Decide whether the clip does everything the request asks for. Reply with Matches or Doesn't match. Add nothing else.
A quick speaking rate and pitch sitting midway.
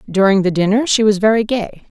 Doesn't match